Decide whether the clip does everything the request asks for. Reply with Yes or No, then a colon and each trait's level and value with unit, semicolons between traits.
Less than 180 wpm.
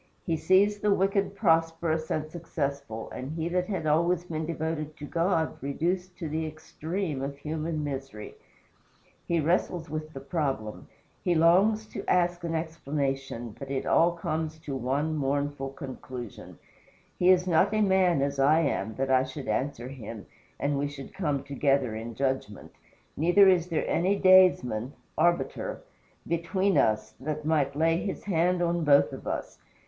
Yes: average, 160 wpm